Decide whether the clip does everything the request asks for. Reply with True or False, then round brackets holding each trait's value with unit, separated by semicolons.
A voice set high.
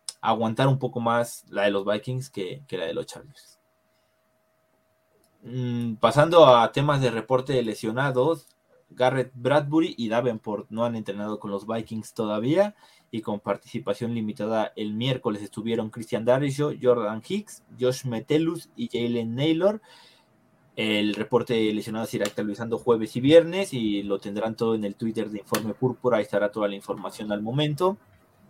False (115 Hz)